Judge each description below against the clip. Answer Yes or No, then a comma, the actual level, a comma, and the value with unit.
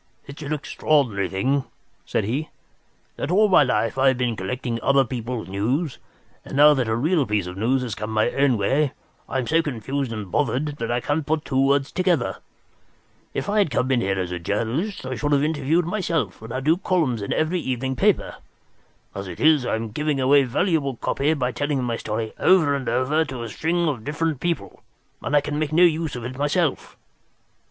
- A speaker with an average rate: No, fast, 210 wpm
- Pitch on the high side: No, low, 135 Hz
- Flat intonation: No, average, 4.6 semitones